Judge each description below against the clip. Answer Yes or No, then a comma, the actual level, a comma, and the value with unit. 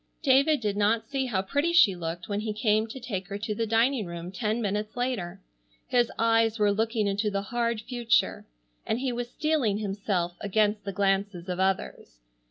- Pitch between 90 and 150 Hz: No, high, 215 Hz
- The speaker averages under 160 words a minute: No, average, 185 wpm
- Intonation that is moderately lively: Yes, average, 3.2 semitones